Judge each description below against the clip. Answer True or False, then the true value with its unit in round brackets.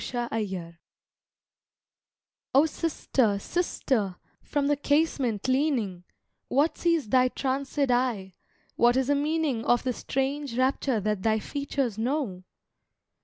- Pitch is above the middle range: True (255 Hz)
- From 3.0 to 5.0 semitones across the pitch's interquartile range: True (4.5 semitones)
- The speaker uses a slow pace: True (120 wpm)